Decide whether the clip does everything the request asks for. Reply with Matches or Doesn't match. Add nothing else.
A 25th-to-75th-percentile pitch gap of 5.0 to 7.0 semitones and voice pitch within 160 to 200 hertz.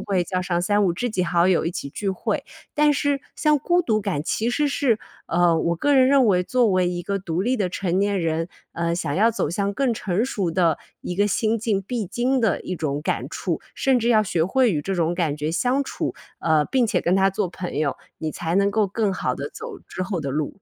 Matches